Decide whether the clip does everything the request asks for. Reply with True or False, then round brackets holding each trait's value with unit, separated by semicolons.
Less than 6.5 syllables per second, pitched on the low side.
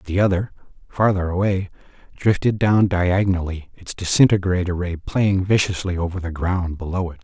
True (5.0 syllables/s; 90 Hz)